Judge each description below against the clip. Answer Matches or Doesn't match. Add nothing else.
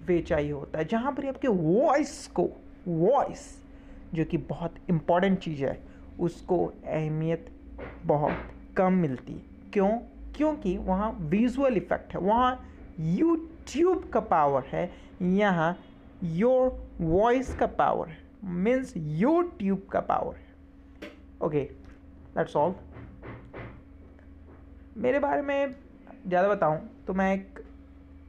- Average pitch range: Doesn't match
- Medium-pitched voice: Matches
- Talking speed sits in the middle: Doesn't match